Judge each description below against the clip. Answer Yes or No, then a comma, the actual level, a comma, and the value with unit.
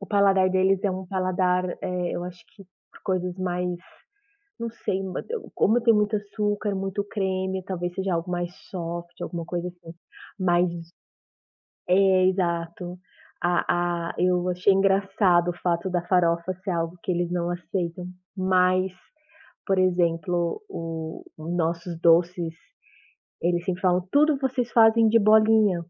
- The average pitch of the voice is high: No, medium, 180 Hz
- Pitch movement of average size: No, narrow, 1.9 semitones